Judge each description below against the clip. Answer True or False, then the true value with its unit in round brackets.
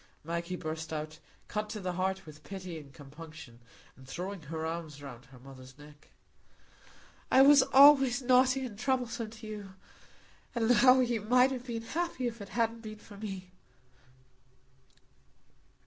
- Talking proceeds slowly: False (150 wpm)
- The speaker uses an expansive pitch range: True (7.4 semitones)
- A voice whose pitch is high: True (200 Hz)